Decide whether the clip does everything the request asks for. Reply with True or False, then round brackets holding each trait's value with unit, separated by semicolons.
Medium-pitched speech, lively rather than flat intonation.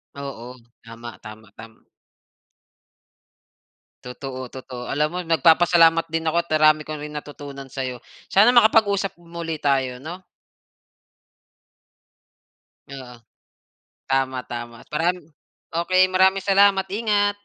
True (155 Hz; 6.1 semitones)